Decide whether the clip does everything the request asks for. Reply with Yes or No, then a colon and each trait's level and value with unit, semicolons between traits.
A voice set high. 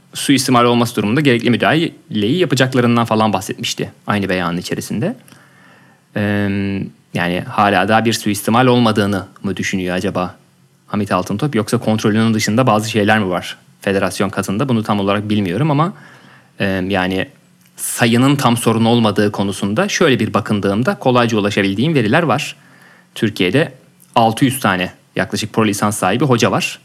No: low, 110 Hz